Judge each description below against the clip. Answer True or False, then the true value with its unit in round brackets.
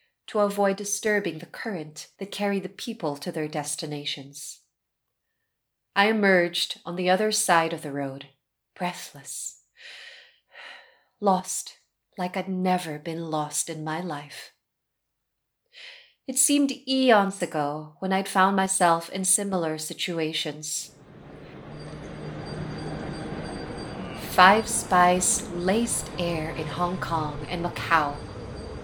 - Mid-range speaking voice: True (180 Hz)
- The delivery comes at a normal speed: False (105 wpm)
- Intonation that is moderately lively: True (4.4 semitones)